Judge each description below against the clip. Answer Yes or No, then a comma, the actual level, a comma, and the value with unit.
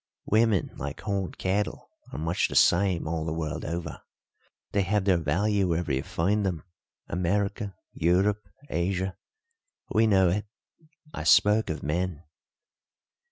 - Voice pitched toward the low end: Yes, very low, 95 Hz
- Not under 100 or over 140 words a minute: Yes, slow, 135 wpm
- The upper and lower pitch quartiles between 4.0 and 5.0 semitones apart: No, average, 3.4 semitones